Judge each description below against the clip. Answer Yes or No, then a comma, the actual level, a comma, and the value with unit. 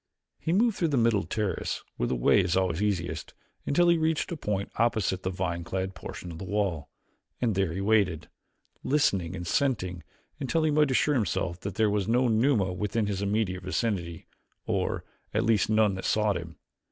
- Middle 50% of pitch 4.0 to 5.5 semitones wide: Yes, average, 4.4 semitones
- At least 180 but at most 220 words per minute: Yes, average, 190 wpm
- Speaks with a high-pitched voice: No, low, 100 Hz